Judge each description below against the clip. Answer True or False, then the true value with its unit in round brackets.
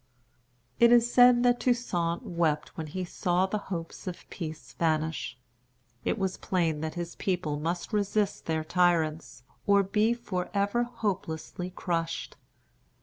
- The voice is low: False (180 Hz)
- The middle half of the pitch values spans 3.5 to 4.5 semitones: True (4.0 semitones)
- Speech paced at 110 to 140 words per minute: True (135 wpm)